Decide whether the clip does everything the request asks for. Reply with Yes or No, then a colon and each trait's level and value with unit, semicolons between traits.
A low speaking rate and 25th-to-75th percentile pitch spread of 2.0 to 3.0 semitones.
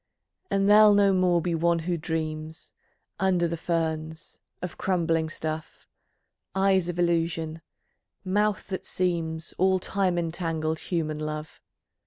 Yes: slow, 125 wpm; narrow, 2.5 semitones